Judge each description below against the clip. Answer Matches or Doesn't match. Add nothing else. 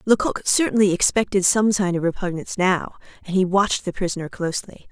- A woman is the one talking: Matches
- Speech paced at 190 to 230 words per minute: Doesn't match